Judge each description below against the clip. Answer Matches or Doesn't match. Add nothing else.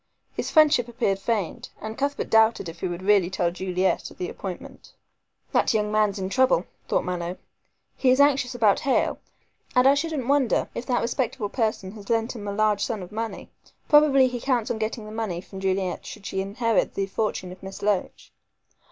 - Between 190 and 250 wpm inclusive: Matches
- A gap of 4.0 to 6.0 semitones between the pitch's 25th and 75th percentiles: Matches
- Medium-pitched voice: Doesn't match